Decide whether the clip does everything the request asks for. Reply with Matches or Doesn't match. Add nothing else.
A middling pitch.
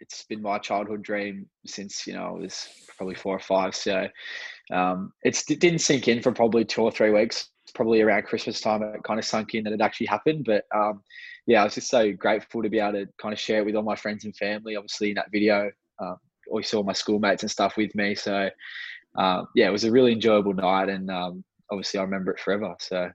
Doesn't match